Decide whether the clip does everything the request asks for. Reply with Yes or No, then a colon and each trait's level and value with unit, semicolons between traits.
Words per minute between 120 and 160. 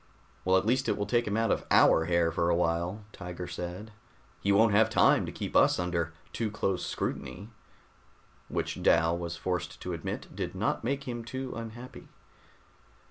No: average, 180 wpm